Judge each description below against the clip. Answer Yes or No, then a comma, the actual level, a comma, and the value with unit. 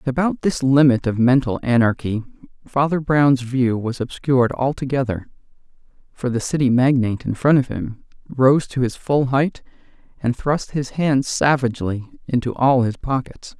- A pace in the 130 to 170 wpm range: Yes, average, 155 wpm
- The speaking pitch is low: Yes, low, 130 Hz